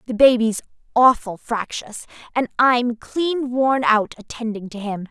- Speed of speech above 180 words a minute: No, average, 140 wpm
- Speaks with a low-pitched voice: No, high, 235 Hz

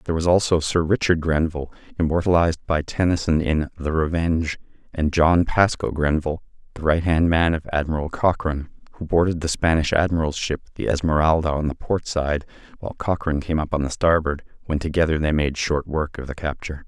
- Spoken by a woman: No, male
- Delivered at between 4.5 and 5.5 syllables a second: No, 5.9 syllables/s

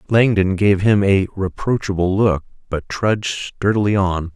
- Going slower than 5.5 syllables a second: Yes, 4.3 syllables/s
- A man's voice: Yes, male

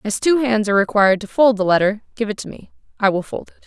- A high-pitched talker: Yes, high, 215 Hz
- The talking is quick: Yes, fast, 280 wpm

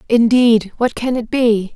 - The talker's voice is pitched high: Yes, high, 230 Hz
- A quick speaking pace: No, average, 170 wpm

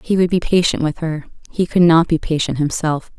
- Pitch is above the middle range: No, medium, 165 Hz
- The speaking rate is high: Yes, fast, 225 wpm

